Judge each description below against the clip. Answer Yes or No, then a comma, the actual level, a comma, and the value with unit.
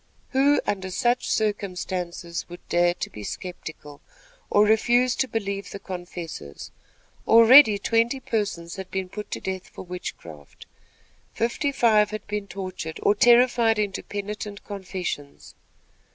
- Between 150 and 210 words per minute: No, slow, 135 wpm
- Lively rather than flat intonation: No, average, 3.9 semitones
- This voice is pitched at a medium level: No, high, 200 Hz